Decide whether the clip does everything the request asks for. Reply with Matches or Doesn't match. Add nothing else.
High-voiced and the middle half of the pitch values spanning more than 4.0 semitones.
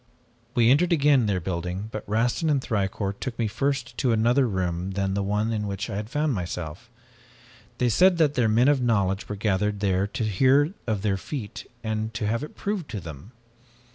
Doesn't match